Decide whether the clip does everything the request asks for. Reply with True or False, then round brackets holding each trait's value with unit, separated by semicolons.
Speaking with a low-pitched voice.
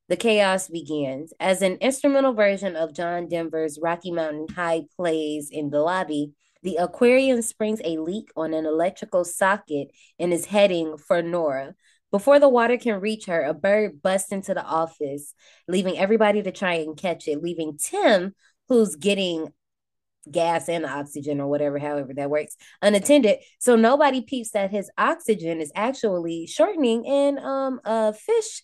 False (180 Hz)